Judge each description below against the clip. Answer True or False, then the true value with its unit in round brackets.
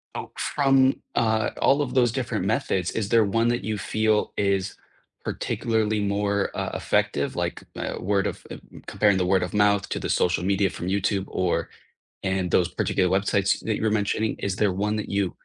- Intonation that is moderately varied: False (2.3 semitones)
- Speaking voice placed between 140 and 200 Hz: False (100 Hz)